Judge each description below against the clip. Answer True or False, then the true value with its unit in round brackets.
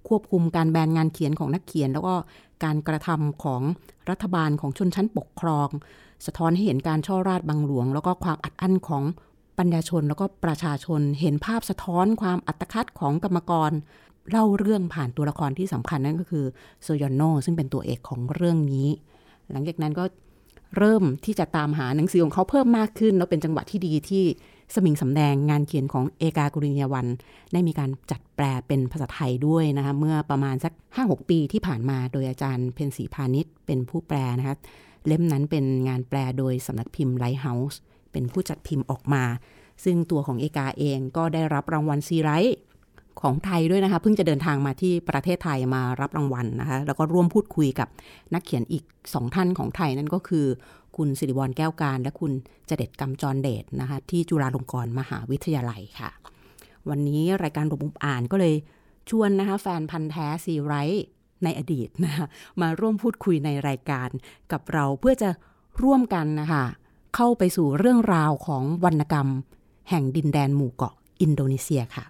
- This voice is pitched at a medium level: True (155 Hz)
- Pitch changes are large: False (4.1 semitones)